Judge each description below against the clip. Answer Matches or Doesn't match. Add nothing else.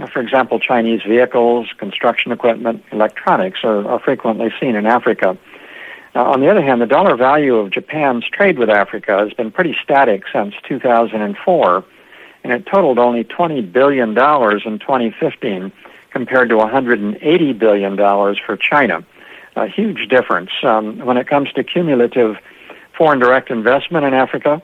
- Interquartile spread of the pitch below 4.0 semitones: Matches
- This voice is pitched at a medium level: Doesn't match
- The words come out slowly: Doesn't match